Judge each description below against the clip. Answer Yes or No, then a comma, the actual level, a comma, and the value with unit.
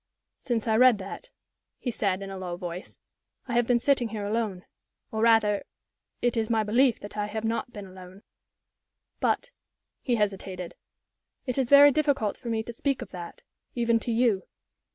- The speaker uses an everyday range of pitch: Yes, average, 3.3 semitones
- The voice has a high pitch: Yes, high, 225 Hz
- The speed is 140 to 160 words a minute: No, average, 175 wpm